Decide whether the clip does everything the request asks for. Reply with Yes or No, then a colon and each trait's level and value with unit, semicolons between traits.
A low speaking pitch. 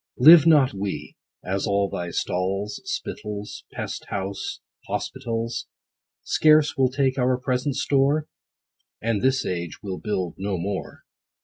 Yes: low, 105 Hz